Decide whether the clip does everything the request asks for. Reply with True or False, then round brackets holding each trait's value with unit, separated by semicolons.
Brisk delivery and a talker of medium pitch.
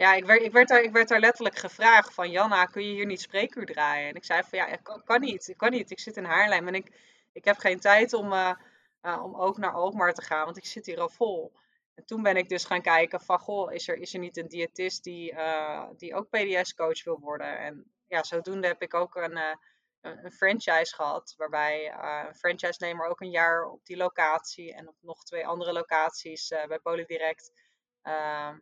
True (225 wpm; 180 Hz)